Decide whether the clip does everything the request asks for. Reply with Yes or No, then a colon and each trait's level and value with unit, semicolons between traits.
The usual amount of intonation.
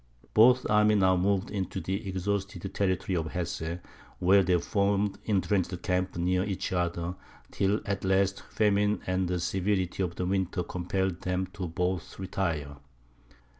No: narrow, 1.8 semitones